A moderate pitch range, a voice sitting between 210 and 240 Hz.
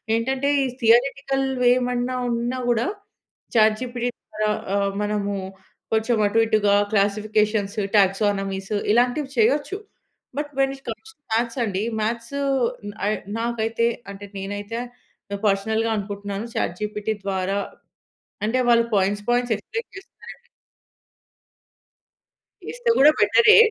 Yes: average, 3.3 semitones; high, 220 Hz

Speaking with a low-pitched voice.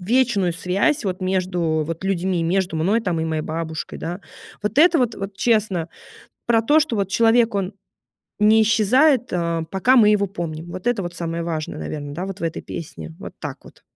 No: high, 190 Hz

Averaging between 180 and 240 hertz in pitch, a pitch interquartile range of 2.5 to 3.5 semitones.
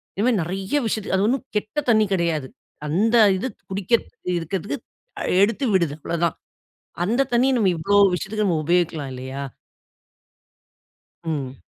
No: high, 190 Hz; average, 5.0 semitones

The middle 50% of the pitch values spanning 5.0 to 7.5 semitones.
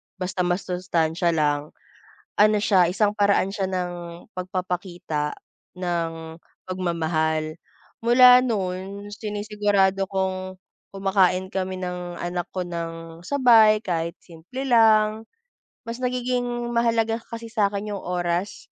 No: average, 3.4 semitones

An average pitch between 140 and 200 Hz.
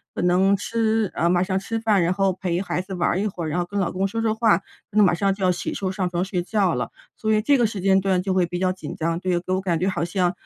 Yes: medium, 185 Hz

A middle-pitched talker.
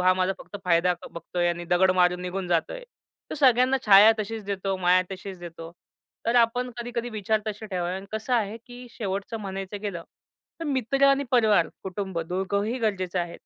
No: high, 200 Hz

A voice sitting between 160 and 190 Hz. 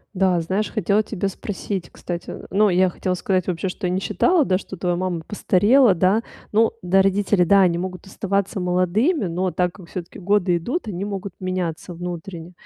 Yes: medium, 185 Hz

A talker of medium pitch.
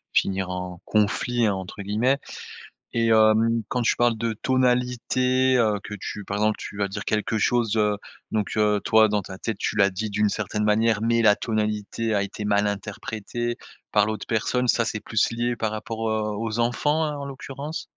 No: low, 110 Hz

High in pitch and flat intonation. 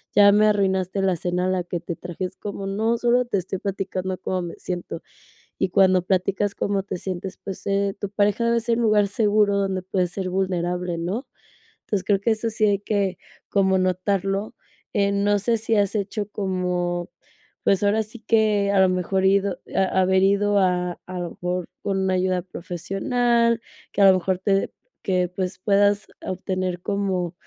Yes: high, 195 Hz; narrow, 1.9 semitones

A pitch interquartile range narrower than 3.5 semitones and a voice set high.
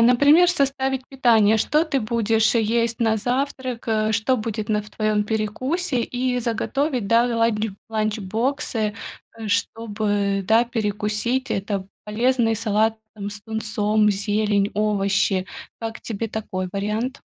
Yes: narrow, 2.6 semitones; high, 220 Hz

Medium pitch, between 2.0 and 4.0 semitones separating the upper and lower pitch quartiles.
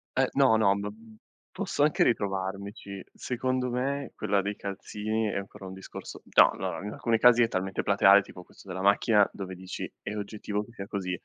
No: low, 100 Hz; narrow, 2.4 semitones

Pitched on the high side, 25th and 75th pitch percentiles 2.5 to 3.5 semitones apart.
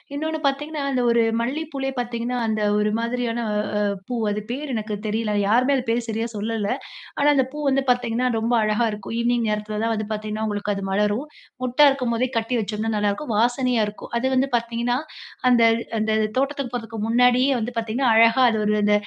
Yes: high, 235 Hz; average, 2.8 semitones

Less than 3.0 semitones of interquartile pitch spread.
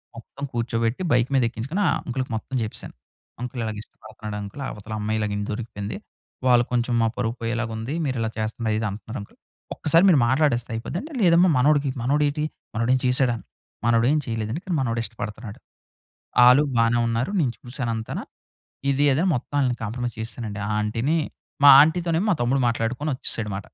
No: average, 3.5 semitones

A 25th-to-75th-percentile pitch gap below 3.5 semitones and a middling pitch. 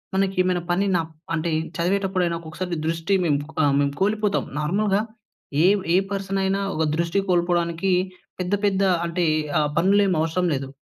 Yes: narrow, 2.6 semitones; medium, 180 Hz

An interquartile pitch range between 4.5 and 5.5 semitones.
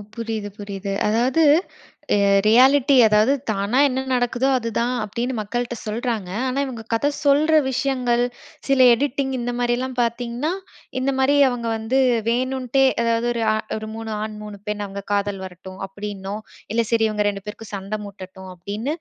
No: average, 3.6 semitones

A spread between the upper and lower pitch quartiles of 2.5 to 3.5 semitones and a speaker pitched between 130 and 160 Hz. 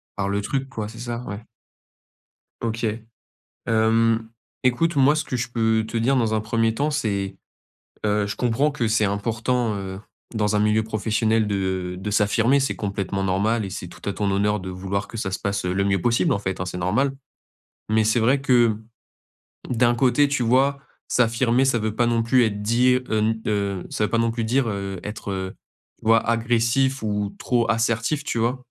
No: average, 2.8 semitones; low, 110 Hz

